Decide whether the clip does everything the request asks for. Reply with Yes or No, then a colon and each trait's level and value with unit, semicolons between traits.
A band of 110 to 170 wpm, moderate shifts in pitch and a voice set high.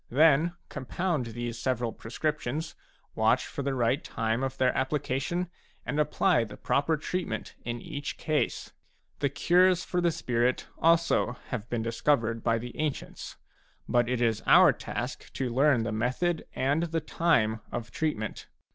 No: average, 150 wpm; average, 5.0 semitones; low, 130 Hz